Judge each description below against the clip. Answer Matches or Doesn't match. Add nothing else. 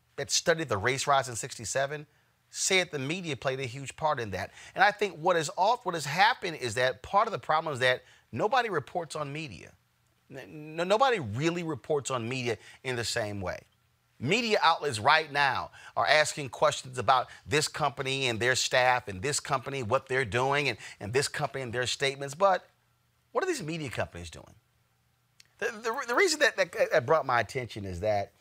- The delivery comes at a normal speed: Matches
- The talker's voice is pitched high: Doesn't match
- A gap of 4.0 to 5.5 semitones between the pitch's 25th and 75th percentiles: Matches